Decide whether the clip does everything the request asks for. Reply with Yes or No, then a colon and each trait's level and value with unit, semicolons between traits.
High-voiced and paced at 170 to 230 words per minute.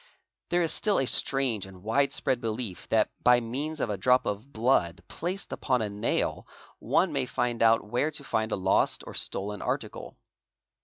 No: low, 120 Hz; average, 185 wpm